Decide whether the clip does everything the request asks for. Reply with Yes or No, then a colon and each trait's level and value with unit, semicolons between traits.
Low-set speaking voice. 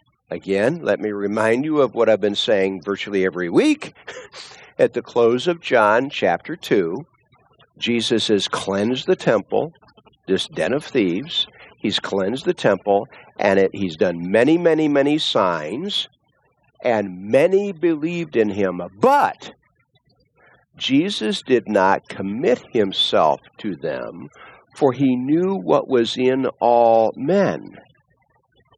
Yes: low, 120 Hz